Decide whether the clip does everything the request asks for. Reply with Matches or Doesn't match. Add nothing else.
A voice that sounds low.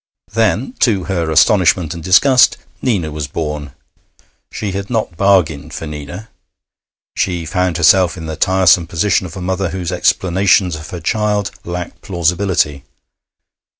Matches